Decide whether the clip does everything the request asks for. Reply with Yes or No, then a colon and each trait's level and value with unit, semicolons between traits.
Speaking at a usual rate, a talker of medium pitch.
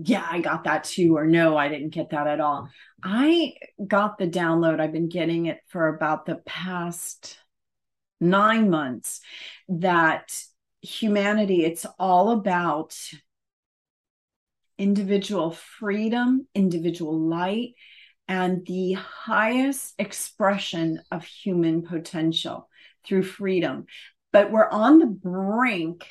No: slow, 115 wpm; medium, 180 Hz